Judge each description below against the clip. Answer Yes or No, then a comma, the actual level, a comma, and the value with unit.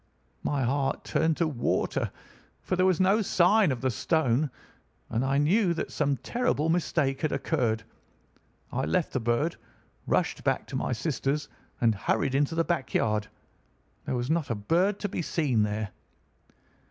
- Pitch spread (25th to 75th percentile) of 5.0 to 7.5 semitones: Yes, wide, 5.5 semitones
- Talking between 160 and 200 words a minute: Yes, average, 165 wpm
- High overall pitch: No, medium, 145 Hz